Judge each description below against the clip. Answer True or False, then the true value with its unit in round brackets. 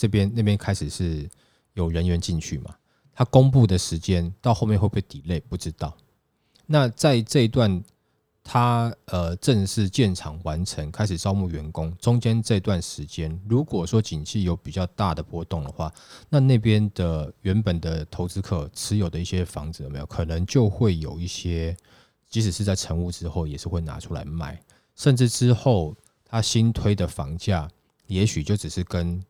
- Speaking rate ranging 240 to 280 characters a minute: True (265 characters per minute)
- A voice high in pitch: False (95 Hz)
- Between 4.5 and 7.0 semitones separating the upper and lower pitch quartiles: True (5.0 semitones)